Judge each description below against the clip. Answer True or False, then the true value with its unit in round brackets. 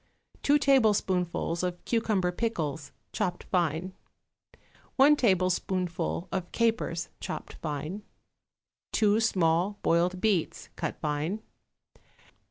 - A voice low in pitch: False (185 Hz)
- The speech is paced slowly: True (90 wpm)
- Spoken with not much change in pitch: False (4.3 semitones)